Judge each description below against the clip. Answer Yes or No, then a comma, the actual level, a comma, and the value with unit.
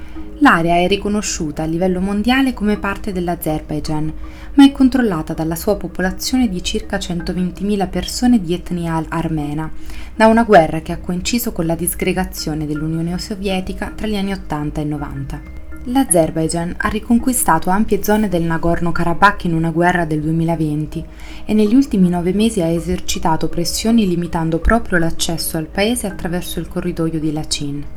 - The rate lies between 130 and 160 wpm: Yes, average, 150 wpm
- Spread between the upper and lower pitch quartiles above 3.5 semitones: Yes, average, 4.1 semitones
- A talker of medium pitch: Yes, medium, 175 Hz